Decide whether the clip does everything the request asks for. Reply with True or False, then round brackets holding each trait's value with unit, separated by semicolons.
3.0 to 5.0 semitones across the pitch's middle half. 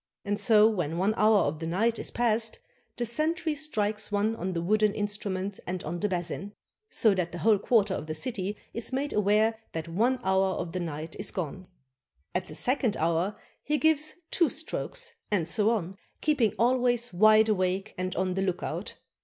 True (4.0 semitones)